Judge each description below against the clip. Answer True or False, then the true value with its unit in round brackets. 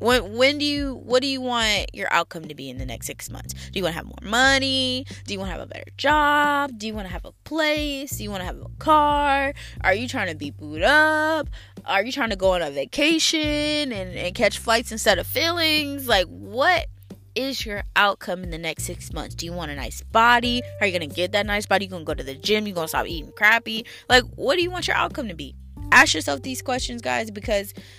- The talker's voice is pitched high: True (220 Hz)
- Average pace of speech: False (250 wpm)